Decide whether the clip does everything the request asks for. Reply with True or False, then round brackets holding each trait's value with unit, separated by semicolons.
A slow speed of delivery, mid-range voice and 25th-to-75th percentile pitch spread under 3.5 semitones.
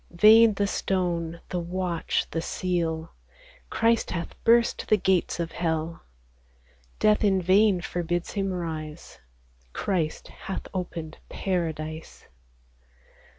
True (110 wpm; 175 Hz; 2.8 semitones)